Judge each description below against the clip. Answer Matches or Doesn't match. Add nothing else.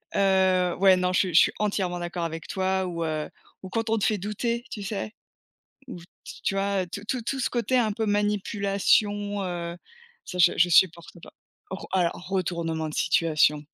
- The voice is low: Doesn't match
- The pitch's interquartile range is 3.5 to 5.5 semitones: Doesn't match